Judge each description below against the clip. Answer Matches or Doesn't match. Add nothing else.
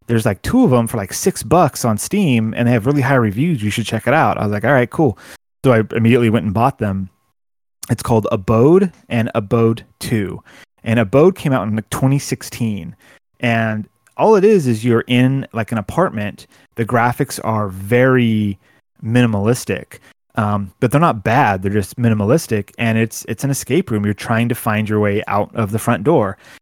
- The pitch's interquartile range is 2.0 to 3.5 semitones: Matches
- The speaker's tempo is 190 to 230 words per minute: Matches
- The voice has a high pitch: Doesn't match